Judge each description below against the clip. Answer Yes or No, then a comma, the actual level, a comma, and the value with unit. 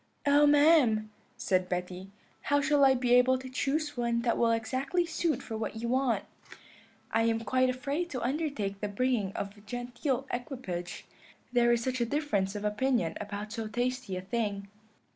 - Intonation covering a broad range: No, average, 4.2 semitones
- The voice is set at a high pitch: Yes, high, 240 Hz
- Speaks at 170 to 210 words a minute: Yes, average, 175 wpm